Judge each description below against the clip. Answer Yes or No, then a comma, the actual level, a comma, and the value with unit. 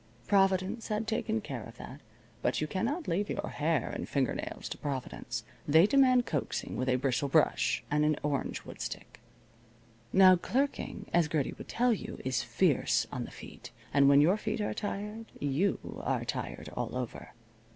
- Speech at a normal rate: Yes, average, 170 wpm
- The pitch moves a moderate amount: No, wide, 7.4 semitones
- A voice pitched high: No, medium, 165 Hz